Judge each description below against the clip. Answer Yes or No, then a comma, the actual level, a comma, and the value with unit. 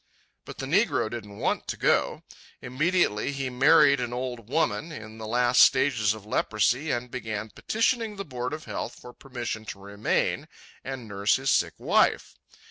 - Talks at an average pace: Yes, average, 165 wpm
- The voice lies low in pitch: Yes, low, 125 Hz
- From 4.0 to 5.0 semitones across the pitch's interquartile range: Yes, average, 4.3 semitones